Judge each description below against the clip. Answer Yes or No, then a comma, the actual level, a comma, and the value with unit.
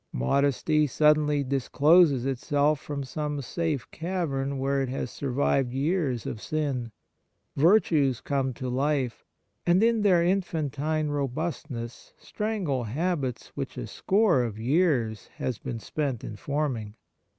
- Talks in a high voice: No, medium, 140 Hz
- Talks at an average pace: No, slow, 130 wpm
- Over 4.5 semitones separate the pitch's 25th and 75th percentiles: No, average, 3.5 semitones